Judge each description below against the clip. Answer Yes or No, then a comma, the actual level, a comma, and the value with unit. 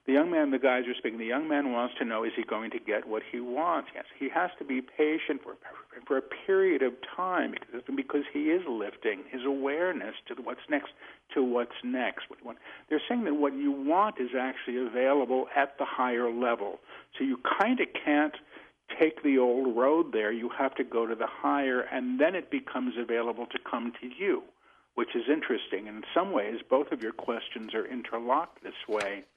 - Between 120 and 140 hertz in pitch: Yes, low, 135 Hz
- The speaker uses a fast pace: Yes, fast, 210 wpm